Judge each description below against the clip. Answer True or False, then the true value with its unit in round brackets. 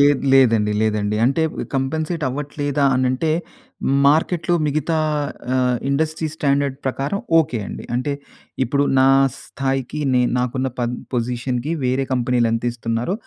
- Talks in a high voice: False (135 Hz)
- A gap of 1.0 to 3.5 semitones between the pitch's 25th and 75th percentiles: True (2.8 semitones)